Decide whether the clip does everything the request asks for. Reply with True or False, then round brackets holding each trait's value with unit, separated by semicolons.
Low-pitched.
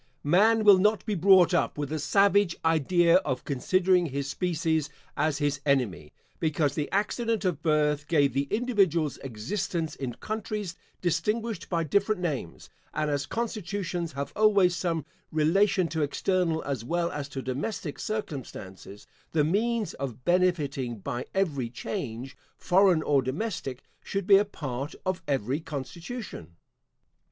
False (165 Hz)